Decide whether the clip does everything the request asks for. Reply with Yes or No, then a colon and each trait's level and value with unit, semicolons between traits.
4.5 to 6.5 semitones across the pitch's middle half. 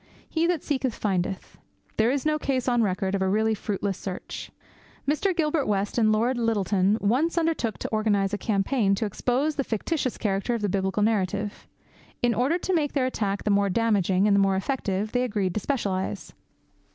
Yes: average, 4.8 semitones